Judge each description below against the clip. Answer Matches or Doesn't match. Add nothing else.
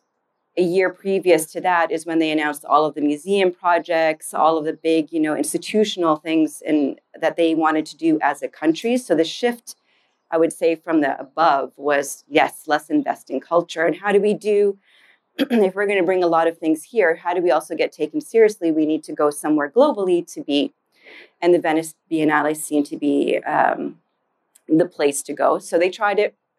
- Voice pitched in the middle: Matches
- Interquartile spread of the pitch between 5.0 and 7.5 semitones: Doesn't match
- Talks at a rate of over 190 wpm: Matches